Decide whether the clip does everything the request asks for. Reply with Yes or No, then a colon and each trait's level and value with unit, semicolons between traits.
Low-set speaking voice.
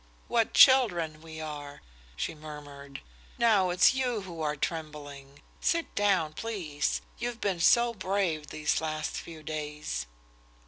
No: medium, 160 Hz